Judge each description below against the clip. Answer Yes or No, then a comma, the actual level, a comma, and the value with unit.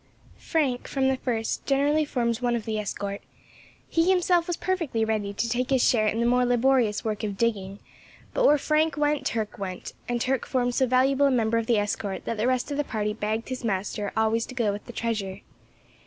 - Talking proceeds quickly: Yes, fast, 215 wpm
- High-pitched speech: Yes, high, 235 Hz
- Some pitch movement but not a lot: Yes, average, 3.8 semitones